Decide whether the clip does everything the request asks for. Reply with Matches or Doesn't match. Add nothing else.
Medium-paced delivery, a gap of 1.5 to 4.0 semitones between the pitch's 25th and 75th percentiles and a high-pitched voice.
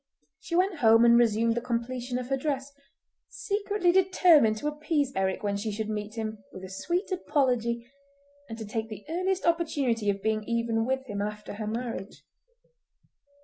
Doesn't match